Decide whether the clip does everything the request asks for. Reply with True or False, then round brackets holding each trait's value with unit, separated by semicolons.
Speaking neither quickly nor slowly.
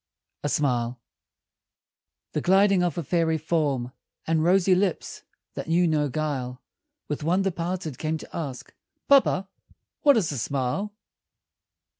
False (130 wpm)